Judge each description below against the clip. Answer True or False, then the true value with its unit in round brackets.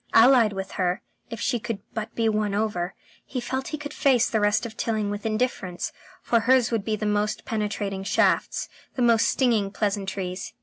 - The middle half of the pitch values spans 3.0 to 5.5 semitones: False (2.6 semitones)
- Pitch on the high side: True (215 Hz)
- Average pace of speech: True (185 wpm)